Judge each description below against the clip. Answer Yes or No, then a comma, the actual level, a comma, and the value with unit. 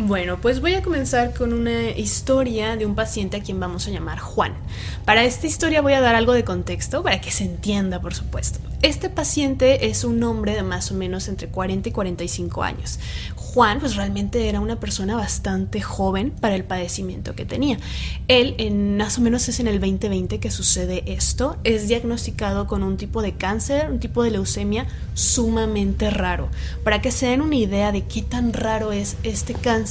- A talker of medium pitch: No, high, 200 Hz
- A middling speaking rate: No, fast, 195 wpm